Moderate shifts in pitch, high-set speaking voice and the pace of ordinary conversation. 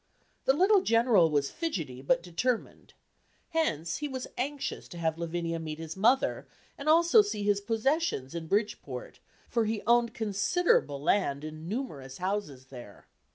No: wide, 8.5 semitones; high, 200 Hz; average, 150 wpm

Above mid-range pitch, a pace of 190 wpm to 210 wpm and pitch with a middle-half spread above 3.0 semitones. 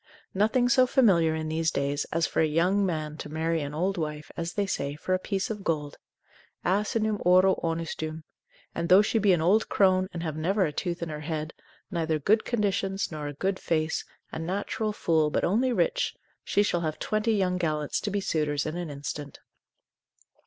No: medium, 170 Hz; average, 195 wpm; average, 4.2 semitones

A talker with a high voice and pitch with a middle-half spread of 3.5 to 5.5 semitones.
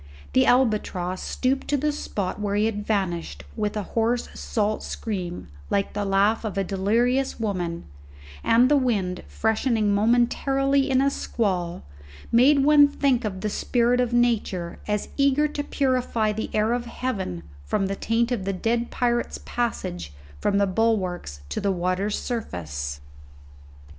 Yes: high, 220 Hz; average, 4.2 semitones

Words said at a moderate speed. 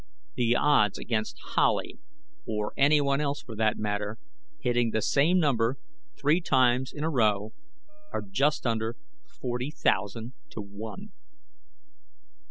No: slow, 125 wpm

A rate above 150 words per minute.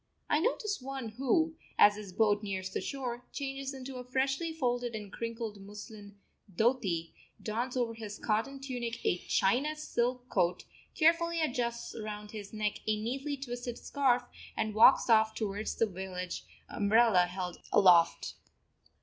No: average, 145 wpm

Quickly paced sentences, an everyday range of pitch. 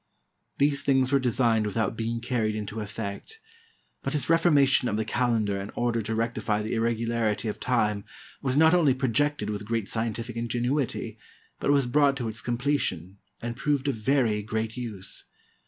No: average, 165 wpm; average, 3.7 semitones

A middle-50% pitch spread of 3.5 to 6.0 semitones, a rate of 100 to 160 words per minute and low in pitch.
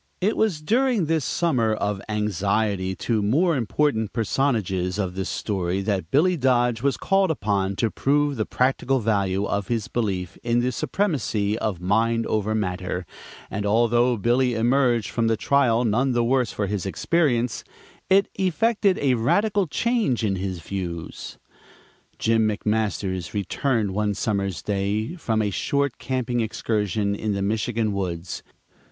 Yes: average, 4.8 semitones; average, 150 wpm; low, 110 Hz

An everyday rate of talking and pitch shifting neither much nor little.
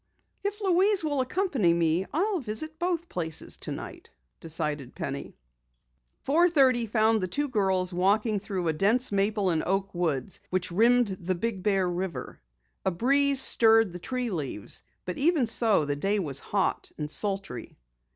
No: average, 155 wpm; wide, 6.5 semitones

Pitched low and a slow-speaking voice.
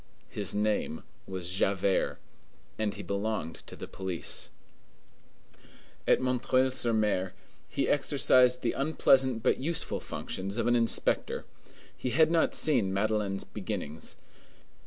Yes: low, 110 Hz; slow, 120 wpm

